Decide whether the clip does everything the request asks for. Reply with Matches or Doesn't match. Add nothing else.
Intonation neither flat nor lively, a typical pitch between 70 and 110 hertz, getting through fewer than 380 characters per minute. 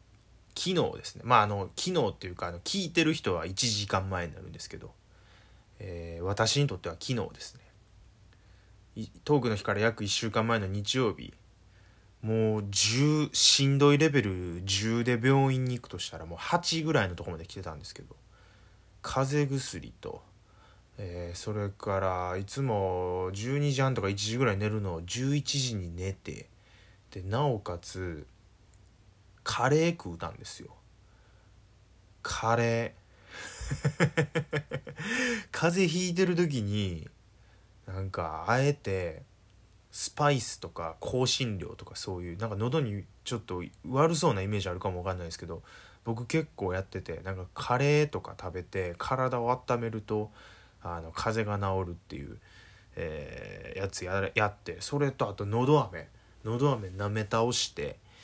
Matches